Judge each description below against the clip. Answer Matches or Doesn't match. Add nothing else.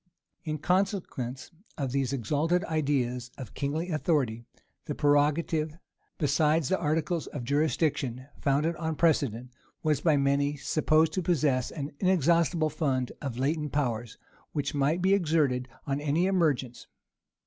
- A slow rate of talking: Matches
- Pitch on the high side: Doesn't match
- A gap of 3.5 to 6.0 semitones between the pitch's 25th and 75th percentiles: Doesn't match